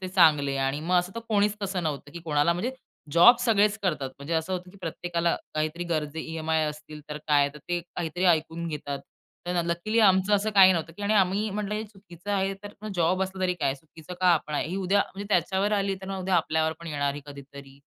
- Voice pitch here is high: No, medium, 175 Hz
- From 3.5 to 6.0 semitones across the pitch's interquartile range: Yes, average, 3.8 semitones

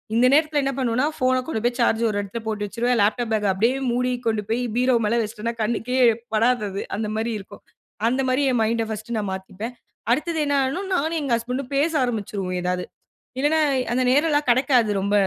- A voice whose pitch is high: Yes, high, 235 Hz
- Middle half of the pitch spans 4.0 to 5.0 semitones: No, average, 3.4 semitones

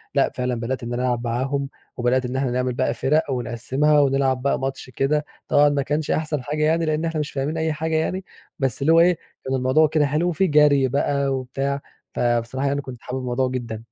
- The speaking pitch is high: No, low, 135 Hz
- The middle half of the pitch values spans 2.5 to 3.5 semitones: Yes, average, 3.1 semitones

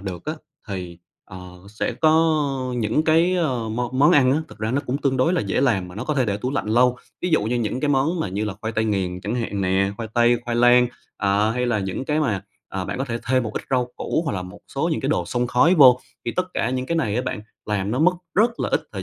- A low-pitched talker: Yes, low, 120 Hz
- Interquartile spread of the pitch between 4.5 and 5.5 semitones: Yes, average, 5.2 semitones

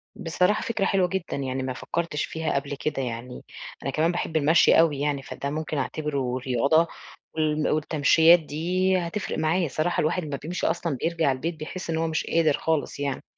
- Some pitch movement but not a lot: Yes, average, 3.1 semitones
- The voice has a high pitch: No, medium, 155 Hz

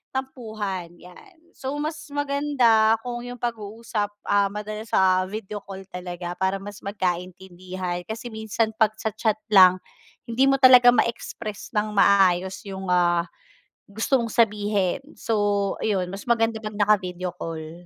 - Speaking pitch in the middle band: No, high, 210 Hz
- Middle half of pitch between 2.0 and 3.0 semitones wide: No, average, 3.6 semitones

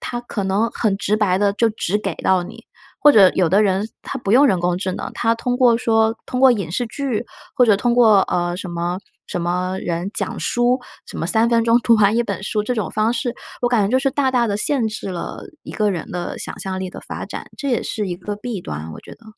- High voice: Yes, high, 215 Hz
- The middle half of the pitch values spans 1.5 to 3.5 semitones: No, average, 4.3 semitones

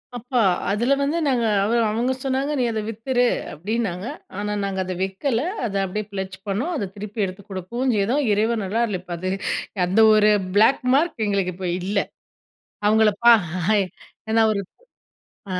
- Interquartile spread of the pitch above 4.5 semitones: No, average, 3.6 semitones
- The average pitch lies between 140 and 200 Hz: No, high, 215 Hz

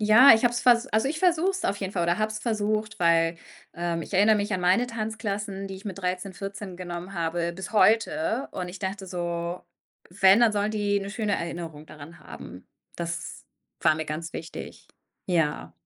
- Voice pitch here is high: Yes, high, 195 Hz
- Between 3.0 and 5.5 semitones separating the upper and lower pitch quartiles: Yes, average, 3.9 semitones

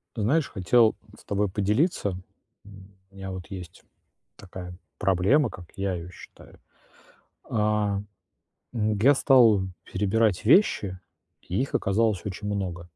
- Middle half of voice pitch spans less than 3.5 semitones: Yes, average, 2.8 semitones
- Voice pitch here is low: Yes, low, 100 Hz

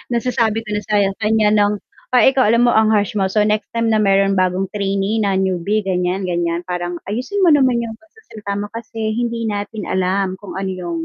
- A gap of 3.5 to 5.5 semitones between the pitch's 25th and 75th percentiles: No, average, 2.9 semitones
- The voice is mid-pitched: No, high, 210 Hz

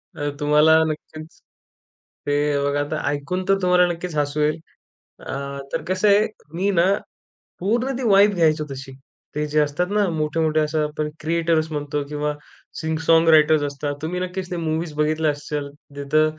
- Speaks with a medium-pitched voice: Yes, medium, 155 Hz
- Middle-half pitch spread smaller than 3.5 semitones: Yes, average, 2.8 semitones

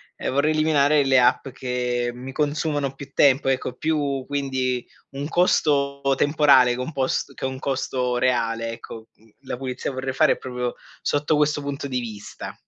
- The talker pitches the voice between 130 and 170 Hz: Yes, low, 135 Hz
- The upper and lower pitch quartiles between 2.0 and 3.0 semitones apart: Yes, narrow, 2.4 semitones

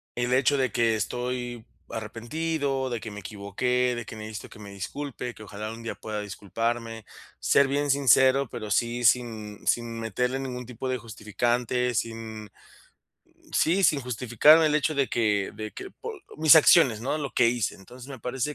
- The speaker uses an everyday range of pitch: Yes, average, 3.3 semitones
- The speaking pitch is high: No, low, 120 Hz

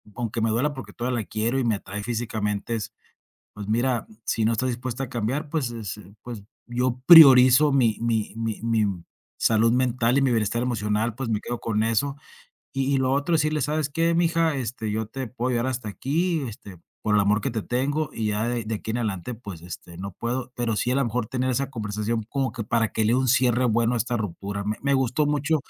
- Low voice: Yes, low, 120 Hz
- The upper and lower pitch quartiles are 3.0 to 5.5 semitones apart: Yes, average, 3.3 semitones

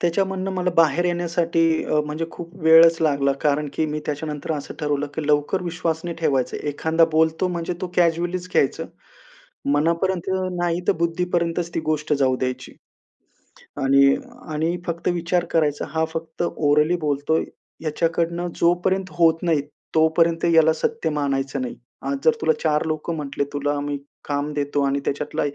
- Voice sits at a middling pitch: Yes, medium, 160 Hz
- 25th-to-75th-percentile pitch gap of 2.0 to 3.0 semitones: Yes, narrow, 2.6 semitones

